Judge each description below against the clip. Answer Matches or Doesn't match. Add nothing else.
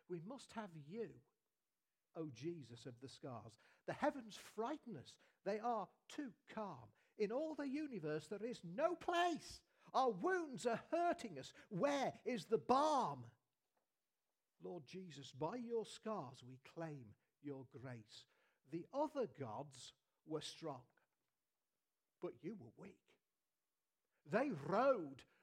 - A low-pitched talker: Doesn't match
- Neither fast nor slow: Doesn't match